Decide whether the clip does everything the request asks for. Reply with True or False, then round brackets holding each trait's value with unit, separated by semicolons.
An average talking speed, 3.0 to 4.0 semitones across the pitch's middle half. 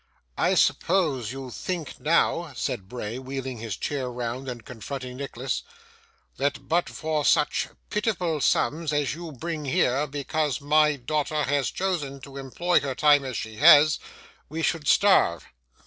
True (150 wpm; 3.3 semitones)